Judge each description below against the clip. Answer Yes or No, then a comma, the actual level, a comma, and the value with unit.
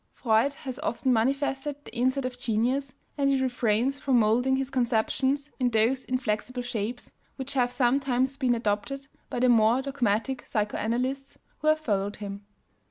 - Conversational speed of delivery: Yes, average, 155 wpm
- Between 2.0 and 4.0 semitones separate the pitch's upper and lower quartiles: Yes, average, 3.1 semitones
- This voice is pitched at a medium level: No, very high, 255 Hz